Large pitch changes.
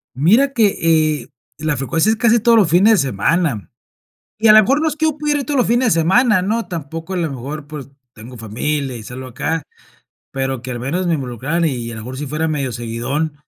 Yes: wide, 8.4 semitones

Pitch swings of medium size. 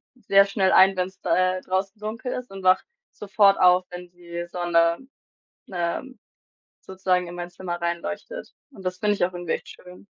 No: narrow, 2.0 semitones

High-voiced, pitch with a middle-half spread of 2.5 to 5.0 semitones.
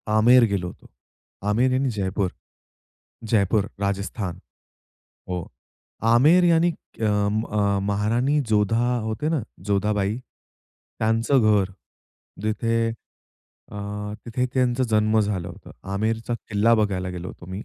No: low, 110 Hz; average, 2.8 semitones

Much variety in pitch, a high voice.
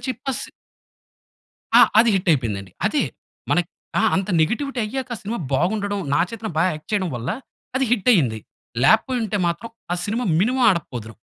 Yes: wide, 6.9 semitones; high, 205 Hz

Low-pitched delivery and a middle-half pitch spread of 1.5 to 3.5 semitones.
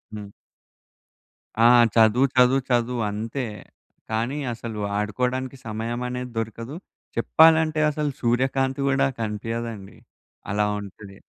Yes: low, 120 Hz; average, 3.2 semitones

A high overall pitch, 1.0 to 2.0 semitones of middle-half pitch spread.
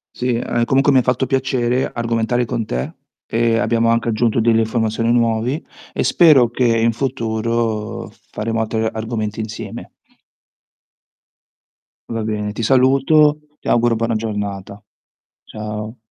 No: low, 115 Hz; narrow, 1.7 semitones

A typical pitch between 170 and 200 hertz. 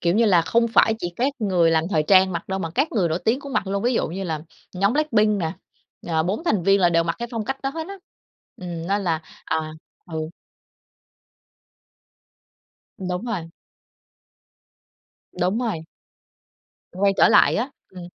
Yes: high, 190 Hz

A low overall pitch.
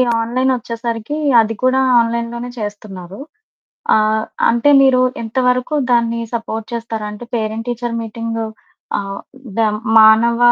No: high, 230 Hz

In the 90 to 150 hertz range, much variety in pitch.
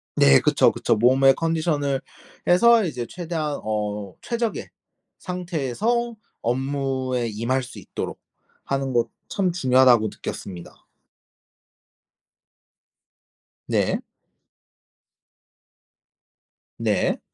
Yes: low, 135 Hz; wide, 6.1 semitones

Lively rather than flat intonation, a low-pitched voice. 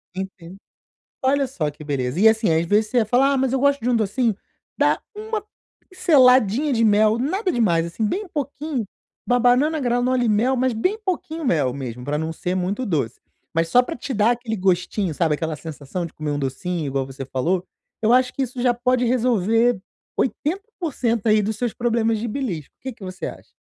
No: wide, 6.6 semitones; high, 225 Hz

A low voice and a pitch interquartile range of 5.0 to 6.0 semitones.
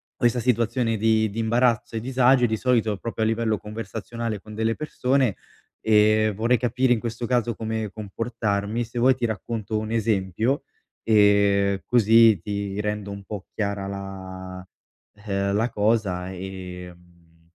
No: low, 110 Hz; average, 2.7 semitones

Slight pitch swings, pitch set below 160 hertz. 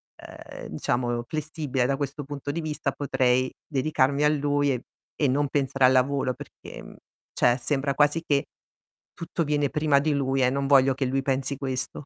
Yes: narrow, 1.9 semitones; medium, 140 Hz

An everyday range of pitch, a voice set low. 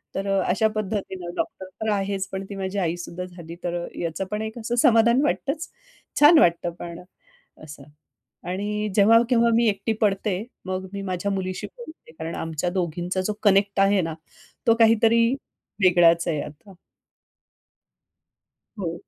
No: average, 3.7 semitones; high, 195 Hz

